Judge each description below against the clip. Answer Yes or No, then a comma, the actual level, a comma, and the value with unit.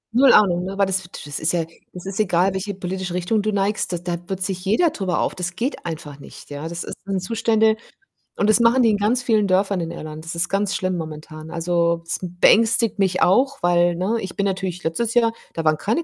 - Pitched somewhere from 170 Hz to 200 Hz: Yes, high, 190 Hz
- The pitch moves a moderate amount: Yes, average, 3.5 semitones